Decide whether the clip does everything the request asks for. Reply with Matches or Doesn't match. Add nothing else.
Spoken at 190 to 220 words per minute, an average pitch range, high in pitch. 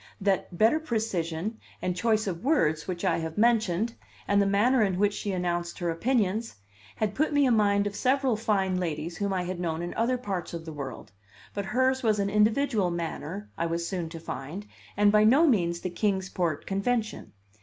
Matches